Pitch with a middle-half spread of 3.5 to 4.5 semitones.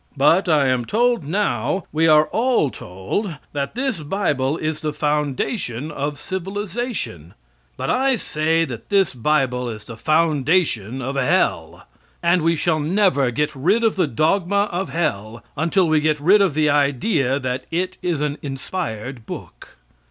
No: wide, 5.6 semitones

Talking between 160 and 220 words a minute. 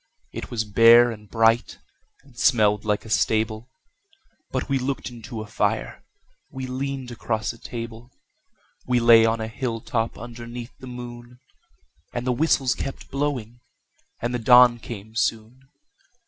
No: average, 145 wpm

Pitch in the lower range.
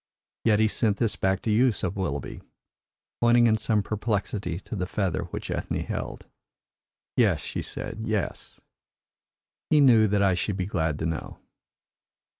Yes: low, 100 Hz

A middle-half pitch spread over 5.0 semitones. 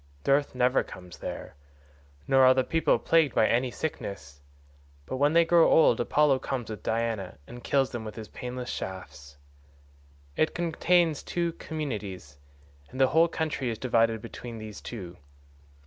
Yes: wide, 5.5 semitones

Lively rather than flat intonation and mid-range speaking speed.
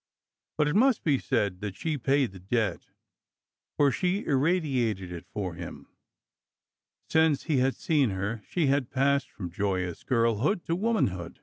Yes: wide, 7.6 semitones; average, 150 wpm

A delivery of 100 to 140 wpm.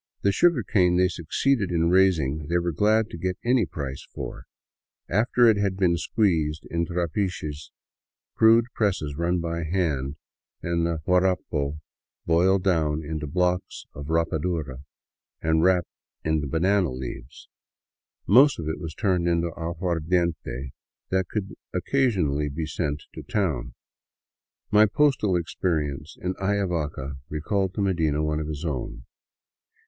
Yes: slow, 135 wpm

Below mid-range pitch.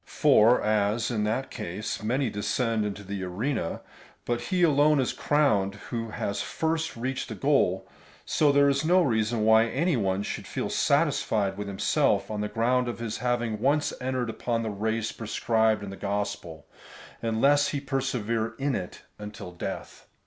Yes: low, 115 Hz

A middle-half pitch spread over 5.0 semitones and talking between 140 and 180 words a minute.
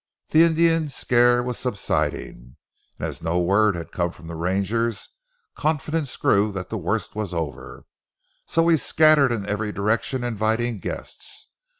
Yes: wide, 5.5 semitones; average, 150 wpm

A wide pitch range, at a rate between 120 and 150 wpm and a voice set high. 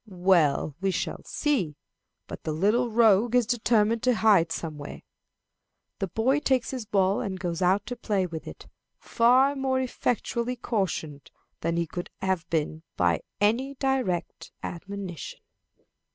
Yes: wide, 5.9 semitones; average, 140 wpm; high, 200 Hz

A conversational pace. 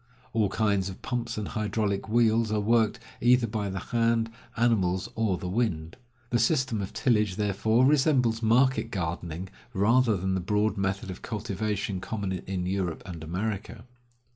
Yes: average, 155 wpm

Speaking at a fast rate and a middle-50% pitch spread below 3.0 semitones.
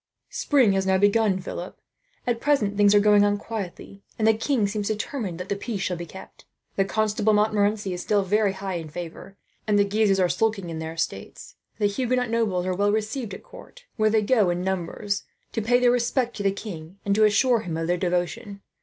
Yes: fast, 215 wpm; narrow, 2.6 semitones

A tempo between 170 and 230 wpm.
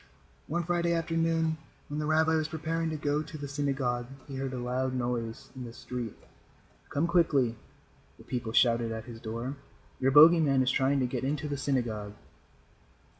Yes: average, 175 wpm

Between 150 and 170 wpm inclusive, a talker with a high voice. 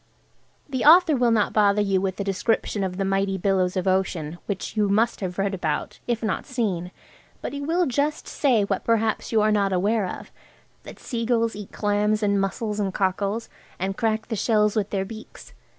No: average, 190 wpm; high, 205 Hz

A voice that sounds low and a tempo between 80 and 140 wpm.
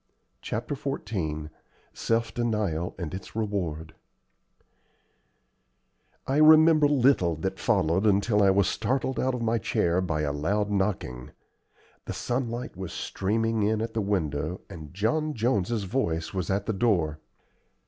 Yes: low, 100 Hz; slow, 135 wpm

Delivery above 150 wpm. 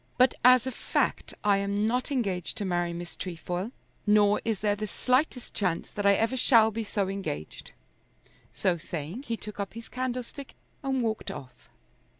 Yes: average, 170 wpm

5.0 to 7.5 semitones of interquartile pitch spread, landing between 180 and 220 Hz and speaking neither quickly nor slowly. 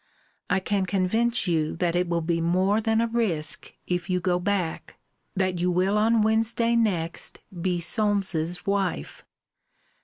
No: average, 3.5 semitones; medium, 185 Hz; average, 150 wpm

